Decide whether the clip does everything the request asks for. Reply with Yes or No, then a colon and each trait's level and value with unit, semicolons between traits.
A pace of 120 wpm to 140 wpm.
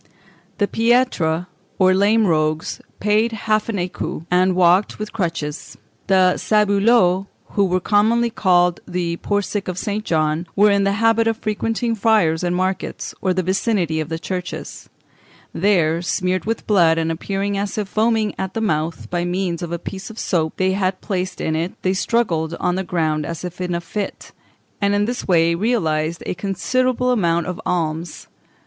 No: average, 175 wpm